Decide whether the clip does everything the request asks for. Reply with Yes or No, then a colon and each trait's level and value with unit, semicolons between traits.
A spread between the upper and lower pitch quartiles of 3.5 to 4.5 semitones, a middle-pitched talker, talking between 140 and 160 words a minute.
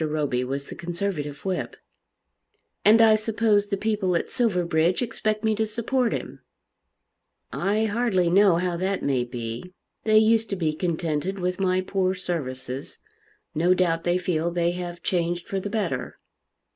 Yes: average, 4.0 semitones; medium, 180 Hz; average, 155 wpm